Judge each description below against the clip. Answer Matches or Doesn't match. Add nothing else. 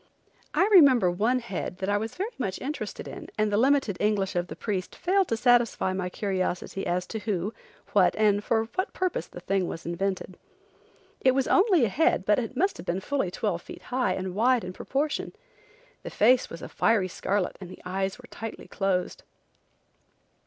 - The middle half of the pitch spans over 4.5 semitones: Matches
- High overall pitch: Matches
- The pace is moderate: Matches